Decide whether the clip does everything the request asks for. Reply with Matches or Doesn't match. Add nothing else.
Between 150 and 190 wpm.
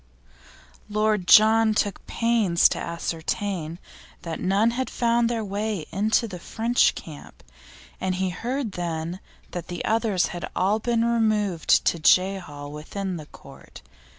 Doesn't match